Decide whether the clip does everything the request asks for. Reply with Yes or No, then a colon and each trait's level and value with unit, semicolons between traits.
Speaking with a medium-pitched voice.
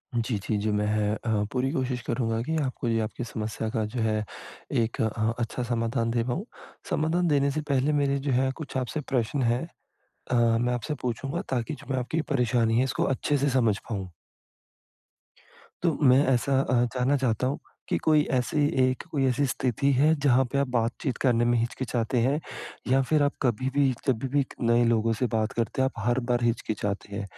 No: low, 125 Hz